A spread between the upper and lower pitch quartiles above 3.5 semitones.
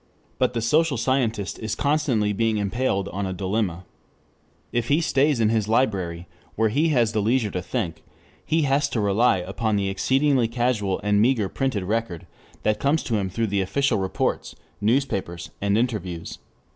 Yes: average, 4.7 semitones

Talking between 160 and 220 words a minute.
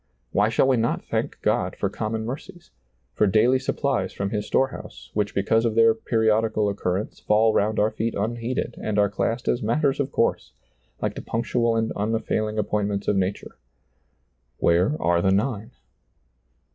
Yes: average, 175 wpm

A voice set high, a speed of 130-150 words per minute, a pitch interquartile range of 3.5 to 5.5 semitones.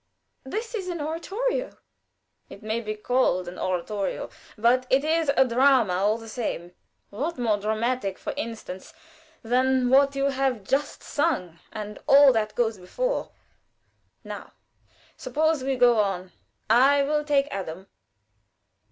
Yes: very high, 250 Hz; average, 140 wpm; average, 5.0 semitones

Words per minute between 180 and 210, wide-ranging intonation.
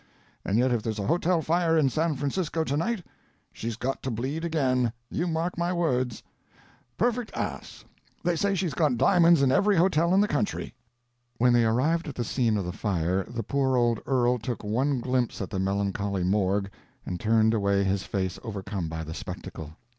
Yes: average, 190 wpm; wide, 7.9 semitones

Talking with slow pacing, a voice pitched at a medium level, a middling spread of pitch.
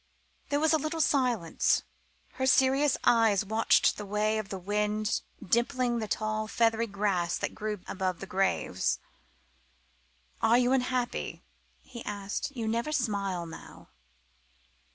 No: slow, 130 wpm; high, 220 Hz; average, 3.7 semitones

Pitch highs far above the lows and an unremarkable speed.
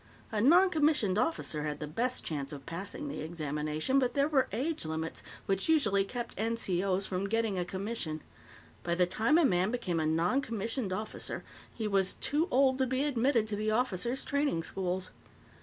Yes: wide, 6.7 semitones; average, 175 wpm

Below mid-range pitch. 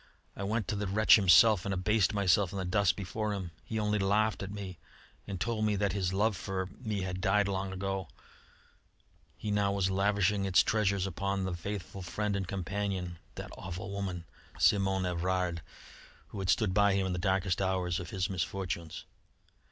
Yes: very low, 95 Hz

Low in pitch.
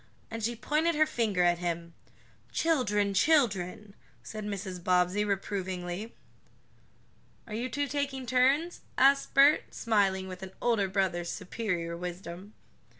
No: high, 205 Hz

